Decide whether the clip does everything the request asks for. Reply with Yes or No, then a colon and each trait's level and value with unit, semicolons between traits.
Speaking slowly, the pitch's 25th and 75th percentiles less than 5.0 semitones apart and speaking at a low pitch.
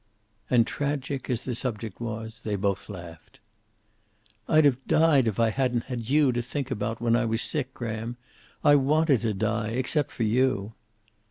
No: average, 170 wpm; average, 3.4 semitones; low, 120 Hz